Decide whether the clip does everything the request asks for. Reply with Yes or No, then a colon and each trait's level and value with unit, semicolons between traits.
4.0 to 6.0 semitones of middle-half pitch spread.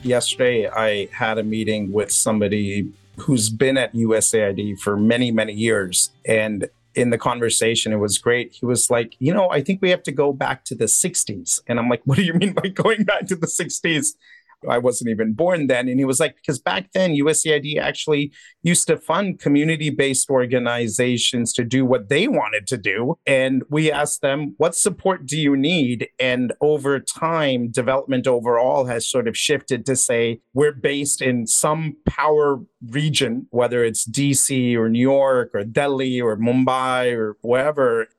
Yes: average, 4.3 semitones